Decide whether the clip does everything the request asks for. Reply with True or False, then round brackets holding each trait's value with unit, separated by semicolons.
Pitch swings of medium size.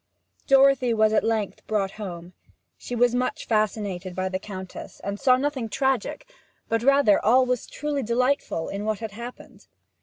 True (4.0 semitones)